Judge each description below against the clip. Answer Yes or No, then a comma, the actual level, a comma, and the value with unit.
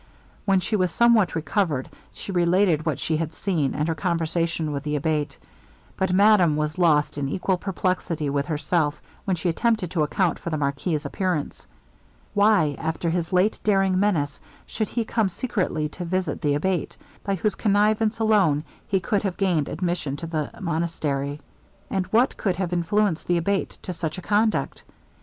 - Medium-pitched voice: Yes, medium, 175 Hz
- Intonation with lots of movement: No, average, 4.1 semitones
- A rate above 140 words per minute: Yes, average, 170 wpm